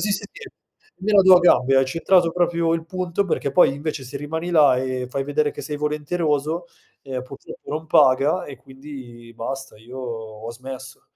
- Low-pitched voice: No, medium, 145 Hz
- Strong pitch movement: No, average, 4.2 semitones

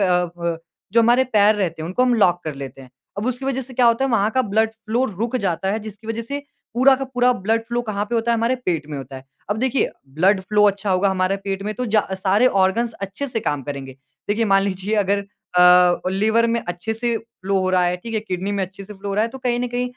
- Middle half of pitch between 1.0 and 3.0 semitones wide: No, average, 3.9 semitones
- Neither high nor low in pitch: No, high, 210 Hz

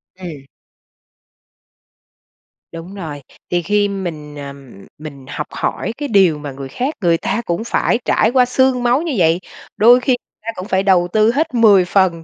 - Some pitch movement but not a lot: No, wide, 6.1 semitones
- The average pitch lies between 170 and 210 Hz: Yes, high, 190 Hz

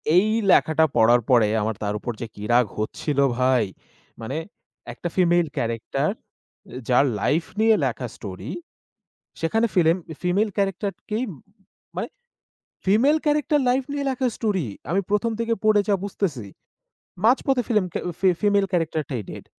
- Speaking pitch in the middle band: Yes, medium, 180 Hz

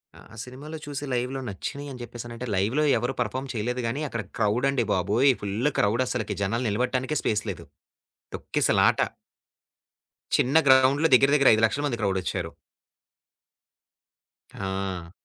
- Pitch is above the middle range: No, low, 120 Hz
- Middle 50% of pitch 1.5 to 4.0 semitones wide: No, average, 4.4 semitones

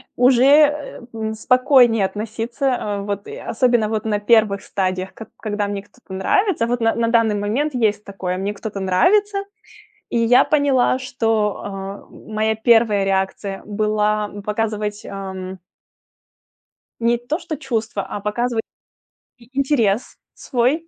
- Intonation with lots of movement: No, average, 3.2 semitones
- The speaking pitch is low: No, high, 220 Hz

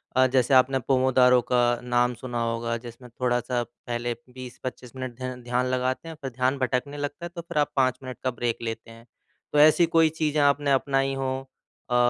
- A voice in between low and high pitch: No, low, 130 Hz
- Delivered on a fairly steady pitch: Yes, narrow, 1.9 semitones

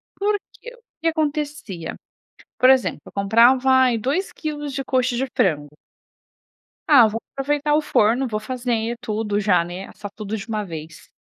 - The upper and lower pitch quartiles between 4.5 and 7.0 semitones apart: Yes, average, 5.3 semitones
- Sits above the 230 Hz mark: Yes, high, 245 Hz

